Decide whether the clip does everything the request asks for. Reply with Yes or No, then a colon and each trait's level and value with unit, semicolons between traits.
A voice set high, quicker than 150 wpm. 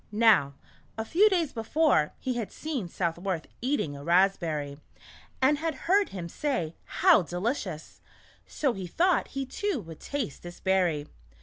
Yes: high, 200 Hz; average, 160 wpm